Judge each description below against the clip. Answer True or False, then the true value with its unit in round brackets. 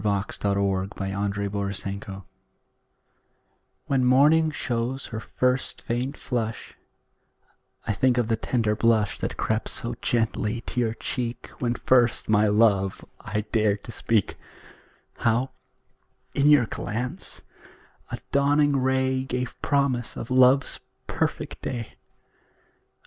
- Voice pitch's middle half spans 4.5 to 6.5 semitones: False (3.5 semitones)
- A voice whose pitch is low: True (115 Hz)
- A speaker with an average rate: False (115 wpm)